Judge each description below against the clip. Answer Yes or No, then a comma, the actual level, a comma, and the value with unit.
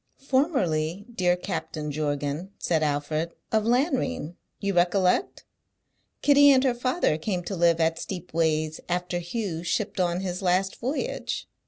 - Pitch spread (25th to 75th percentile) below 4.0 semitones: No, average, 5.3 semitones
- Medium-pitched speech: Yes, medium, 180 Hz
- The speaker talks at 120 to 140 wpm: Yes, slow, 135 wpm